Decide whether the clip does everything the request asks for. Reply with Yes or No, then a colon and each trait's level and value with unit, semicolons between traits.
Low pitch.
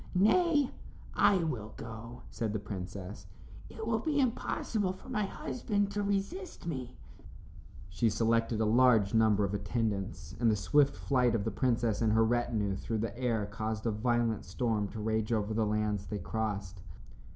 Yes: low, 115 Hz